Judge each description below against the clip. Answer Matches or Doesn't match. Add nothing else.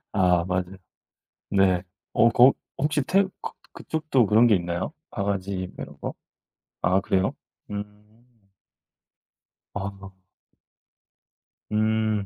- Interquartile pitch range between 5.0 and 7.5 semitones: Doesn't match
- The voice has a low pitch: Matches